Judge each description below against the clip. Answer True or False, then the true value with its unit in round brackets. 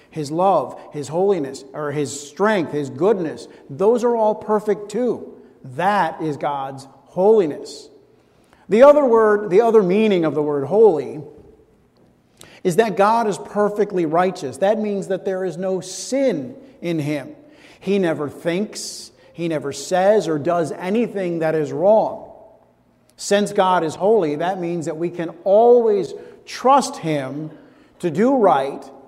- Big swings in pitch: True (6.2 semitones)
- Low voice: False (190 Hz)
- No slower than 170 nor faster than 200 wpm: False (145 wpm)